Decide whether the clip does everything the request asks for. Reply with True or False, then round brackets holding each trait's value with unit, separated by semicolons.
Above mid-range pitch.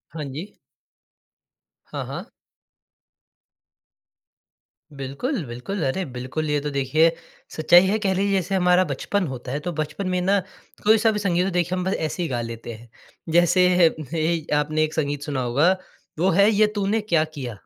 False (165 Hz)